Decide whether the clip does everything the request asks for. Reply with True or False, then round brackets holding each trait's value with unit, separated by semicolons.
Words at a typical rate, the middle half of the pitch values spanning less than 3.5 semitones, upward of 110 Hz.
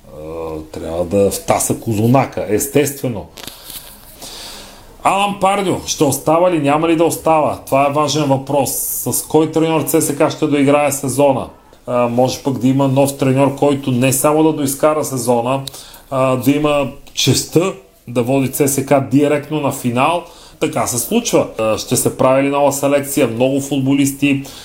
True (140 wpm; 2.4 semitones; 140 Hz)